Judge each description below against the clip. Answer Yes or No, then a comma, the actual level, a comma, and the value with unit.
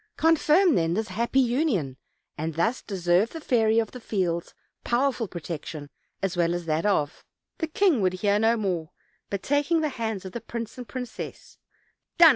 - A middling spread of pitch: No, wide, 6.6 semitones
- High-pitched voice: Yes, high, 220 Hz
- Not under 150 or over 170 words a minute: No, average, 185 wpm